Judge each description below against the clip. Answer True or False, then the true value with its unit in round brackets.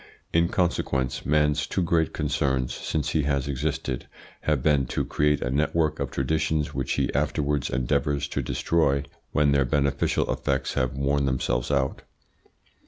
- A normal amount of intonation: False (2.3 semitones)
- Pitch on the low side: True (70 Hz)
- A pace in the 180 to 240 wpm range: False (150 wpm)